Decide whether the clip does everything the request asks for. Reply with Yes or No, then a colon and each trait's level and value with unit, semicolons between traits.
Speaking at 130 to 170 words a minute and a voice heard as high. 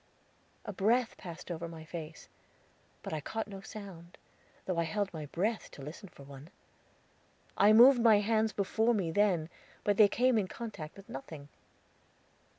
Yes: average, 160 wpm; high, 195 Hz